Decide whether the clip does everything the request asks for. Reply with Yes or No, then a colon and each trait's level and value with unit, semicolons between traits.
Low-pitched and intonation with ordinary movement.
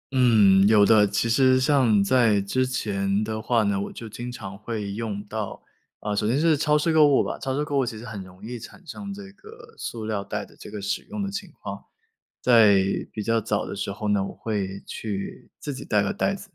Yes: low, 110 Hz; average, 4.6 semitones